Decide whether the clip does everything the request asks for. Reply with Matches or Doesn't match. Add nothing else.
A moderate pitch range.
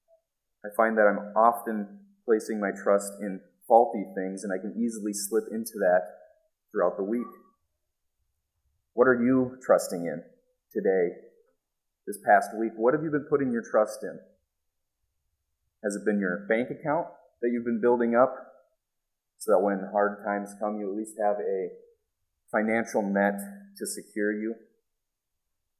Matches